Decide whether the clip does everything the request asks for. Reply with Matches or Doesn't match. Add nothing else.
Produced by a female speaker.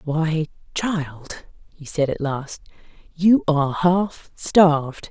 Matches